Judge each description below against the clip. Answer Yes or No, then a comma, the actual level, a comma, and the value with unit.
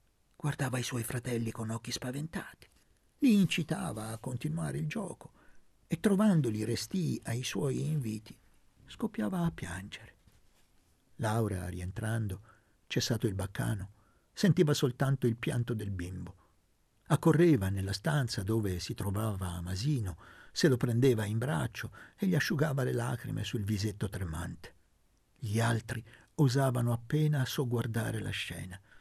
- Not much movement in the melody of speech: No, wide, 5.6 semitones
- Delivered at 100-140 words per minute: Yes, average, 125 wpm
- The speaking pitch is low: Yes, low, 115 Hz